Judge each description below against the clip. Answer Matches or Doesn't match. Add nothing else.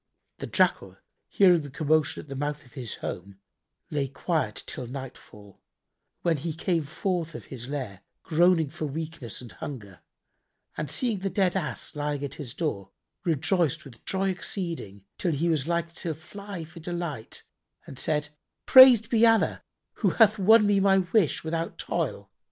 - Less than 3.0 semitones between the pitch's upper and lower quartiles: Doesn't match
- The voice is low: Doesn't match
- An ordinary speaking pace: Matches